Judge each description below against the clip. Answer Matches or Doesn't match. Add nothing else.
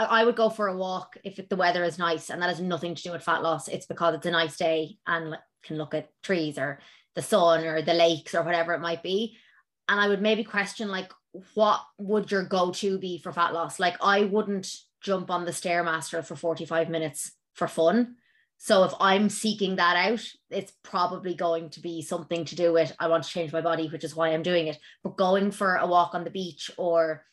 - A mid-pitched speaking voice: Matches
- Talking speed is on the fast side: Matches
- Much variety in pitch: Doesn't match